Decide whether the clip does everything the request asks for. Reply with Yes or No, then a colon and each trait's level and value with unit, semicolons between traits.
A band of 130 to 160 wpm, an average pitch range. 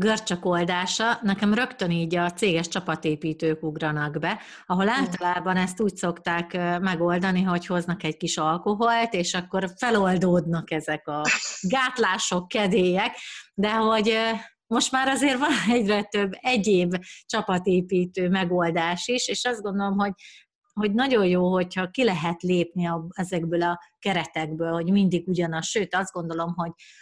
Yes: average, 140 wpm; average, 3.4 semitones